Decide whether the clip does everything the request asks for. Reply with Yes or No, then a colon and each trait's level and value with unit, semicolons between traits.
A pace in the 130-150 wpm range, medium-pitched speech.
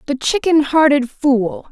No: average, 140 wpm; very high, 280 Hz